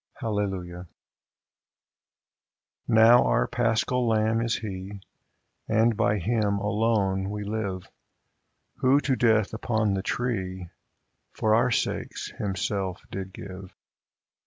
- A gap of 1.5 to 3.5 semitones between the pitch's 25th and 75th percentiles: Yes, average, 2.9 semitones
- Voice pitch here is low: Yes, low, 105 Hz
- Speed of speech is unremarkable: No, slow, 105 wpm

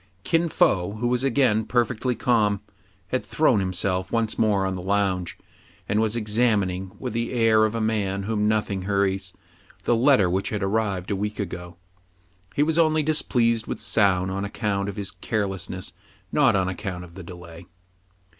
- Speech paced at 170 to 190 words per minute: Yes, average, 175 wpm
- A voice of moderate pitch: No, low, 105 Hz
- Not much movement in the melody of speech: No, average, 3.4 semitones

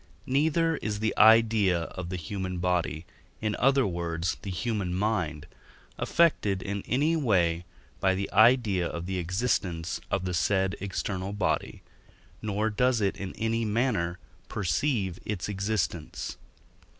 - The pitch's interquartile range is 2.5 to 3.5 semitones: No, average, 3.9 semitones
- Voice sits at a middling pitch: No, low, 100 Hz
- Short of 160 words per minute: Yes, slow, 135 wpm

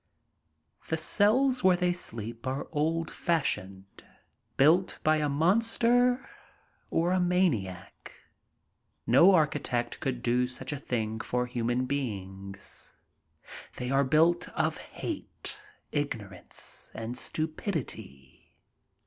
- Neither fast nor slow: No, slow, 105 wpm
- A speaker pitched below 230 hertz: Yes, medium, 140 Hz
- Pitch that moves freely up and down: Yes, wide, 6.6 semitones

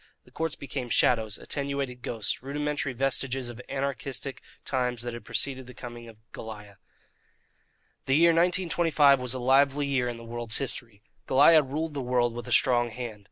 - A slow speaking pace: No, average, 170 wpm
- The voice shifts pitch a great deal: No, average, 2.9 semitones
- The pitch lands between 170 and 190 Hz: No, low, 130 Hz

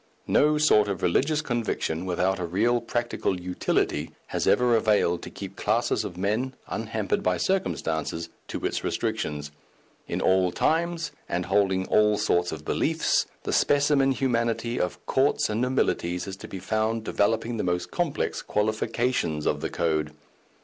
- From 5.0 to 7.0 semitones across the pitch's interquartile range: Yes, wide, 5.4 semitones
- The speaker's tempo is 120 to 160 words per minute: Yes, average, 150 wpm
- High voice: No, low, 105 Hz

